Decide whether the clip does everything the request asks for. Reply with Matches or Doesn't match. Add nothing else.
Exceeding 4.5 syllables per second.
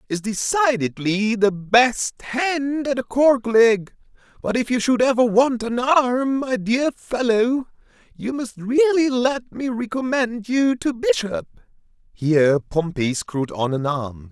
Doesn't match